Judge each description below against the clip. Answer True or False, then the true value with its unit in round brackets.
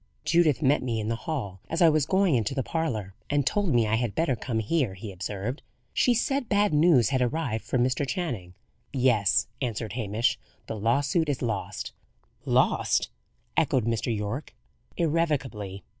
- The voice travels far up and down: True (6.2 semitones)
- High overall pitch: False (125 Hz)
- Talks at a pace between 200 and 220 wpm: False (165 wpm)